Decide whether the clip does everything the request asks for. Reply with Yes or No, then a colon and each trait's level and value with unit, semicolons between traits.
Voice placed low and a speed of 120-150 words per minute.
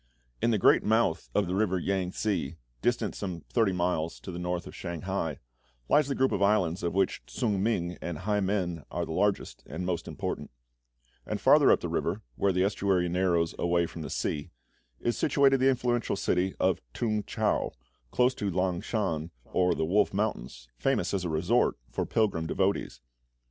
No: very low, 95 Hz; average, 185 wpm